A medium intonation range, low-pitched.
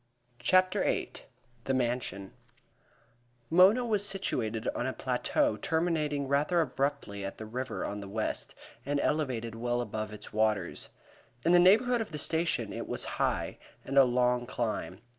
No: wide, 7.0 semitones; low, 130 Hz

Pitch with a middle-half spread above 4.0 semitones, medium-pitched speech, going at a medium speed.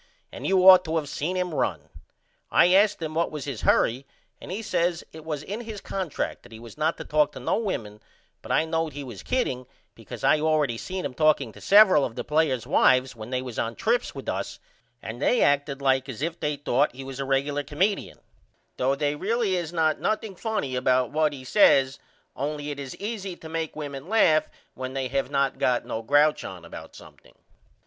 No: average, 4.8 semitones; medium, 150 Hz; fast, 215 wpm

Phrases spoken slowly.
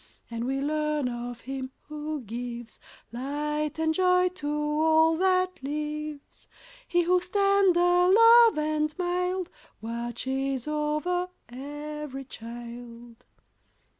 Yes: slow, 105 wpm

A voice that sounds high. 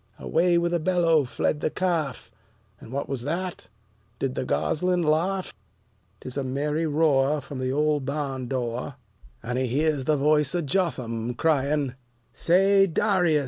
No: medium, 150 Hz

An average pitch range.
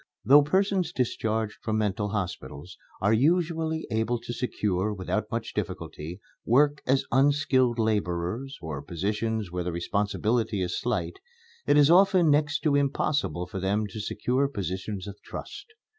No: wide, 6.3 semitones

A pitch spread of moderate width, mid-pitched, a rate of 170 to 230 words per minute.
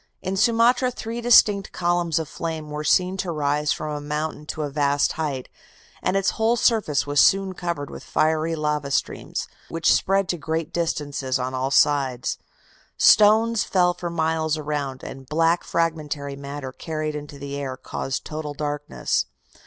No: average, 3.4 semitones; medium, 155 Hz; average, 160 wpm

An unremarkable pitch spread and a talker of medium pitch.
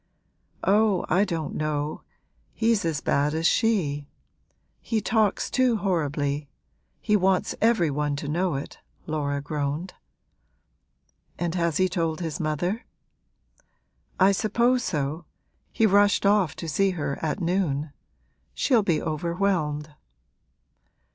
Yes: average, 5.0 semitones; medium, 170 Hz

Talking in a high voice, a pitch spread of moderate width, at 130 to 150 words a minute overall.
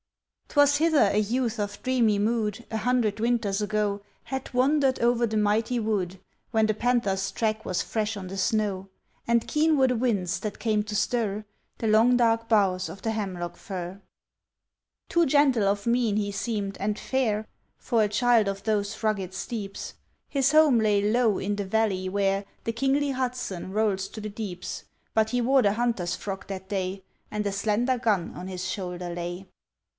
No: high, 215 Hz; average, 3.3 semitones; average, 180 wpm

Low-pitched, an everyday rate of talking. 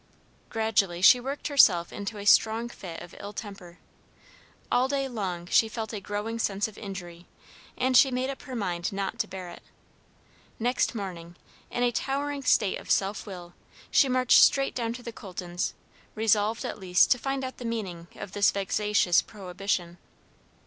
No: high, 210 Hz; average, 170 wpm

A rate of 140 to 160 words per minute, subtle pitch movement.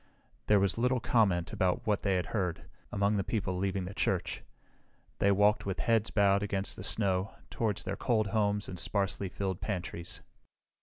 No: average, 170 wpm; narrow, 2.0 semitones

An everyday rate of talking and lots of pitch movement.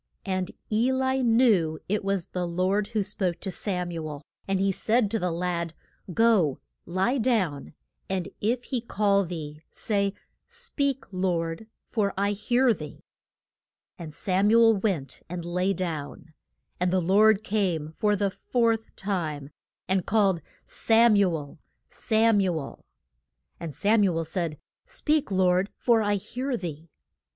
No: average, 155 wpm; average, 4.3 semitones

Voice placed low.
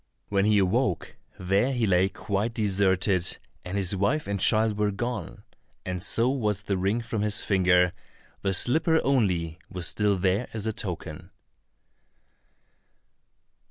Yes: low, 100 Hz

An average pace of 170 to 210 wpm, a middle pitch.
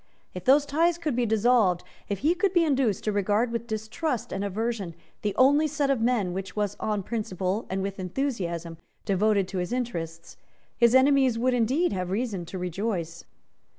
No: average, 180 wpm; high, 220 Hz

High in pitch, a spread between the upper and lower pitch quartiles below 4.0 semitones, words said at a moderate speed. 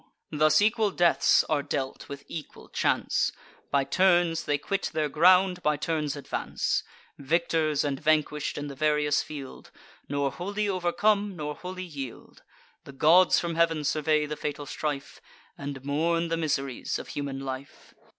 No: medium, 155 Hz; average, 3.3 semitones; average, 150 wpm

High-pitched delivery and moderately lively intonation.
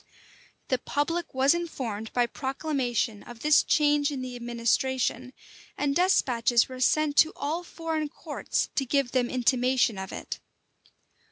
Yes: very high, 260 Hz; average, 3.5 semitones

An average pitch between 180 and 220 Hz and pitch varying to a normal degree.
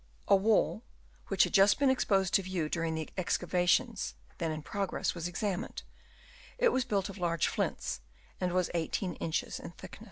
Yes: medium, 185 Hz; average, 3.1 semitones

